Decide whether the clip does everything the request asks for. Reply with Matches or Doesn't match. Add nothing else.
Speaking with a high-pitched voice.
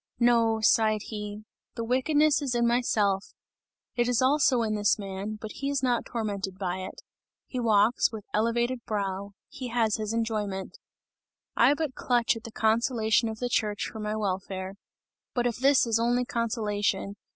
Matches